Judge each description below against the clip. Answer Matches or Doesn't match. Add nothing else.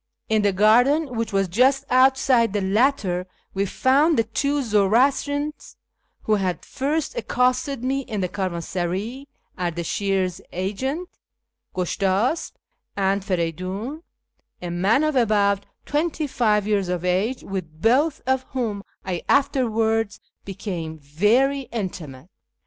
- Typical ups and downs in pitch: Doesn't match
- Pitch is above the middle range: Matches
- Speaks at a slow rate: Matches